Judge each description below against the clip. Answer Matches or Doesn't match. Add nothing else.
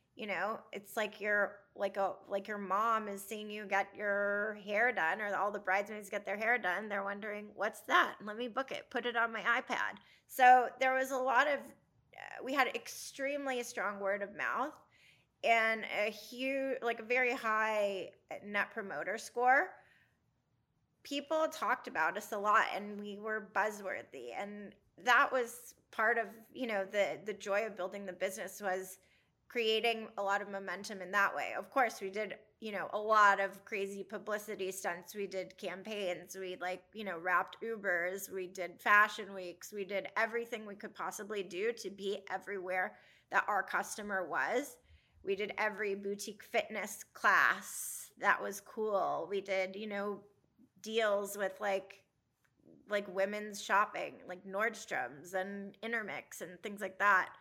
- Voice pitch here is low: Doesn't match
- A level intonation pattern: Matches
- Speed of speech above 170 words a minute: Doesn't match